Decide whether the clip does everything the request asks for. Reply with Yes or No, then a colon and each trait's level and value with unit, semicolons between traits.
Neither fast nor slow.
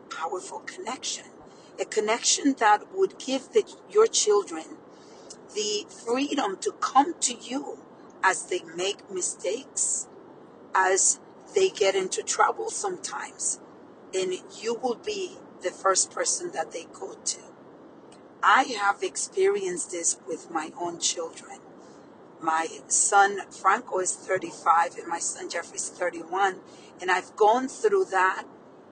No: slow, 125 wpm